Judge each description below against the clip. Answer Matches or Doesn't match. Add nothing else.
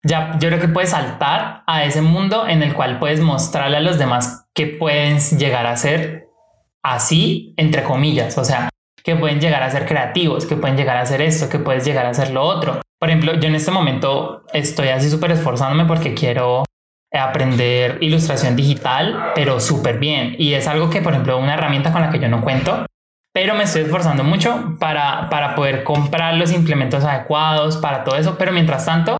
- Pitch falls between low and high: Matches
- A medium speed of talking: Doesn't match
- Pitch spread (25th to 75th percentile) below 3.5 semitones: Matches